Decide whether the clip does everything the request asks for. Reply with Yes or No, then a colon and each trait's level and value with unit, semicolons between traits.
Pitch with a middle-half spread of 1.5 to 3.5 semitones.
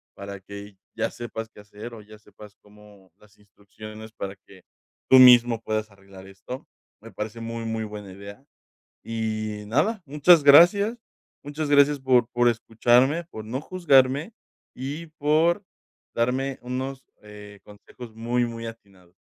No: average, 4.4 semitones